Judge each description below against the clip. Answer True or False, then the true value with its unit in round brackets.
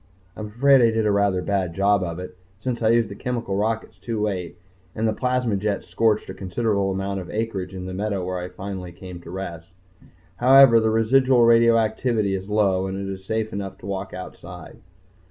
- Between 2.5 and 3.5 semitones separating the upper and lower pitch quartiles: True (3.0 semitones)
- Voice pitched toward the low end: True (100 Hz)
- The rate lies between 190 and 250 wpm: True (200 wpm)